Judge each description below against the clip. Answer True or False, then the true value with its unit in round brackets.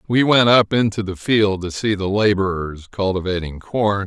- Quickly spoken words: False (175 wpm)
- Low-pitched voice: True (100 Hz)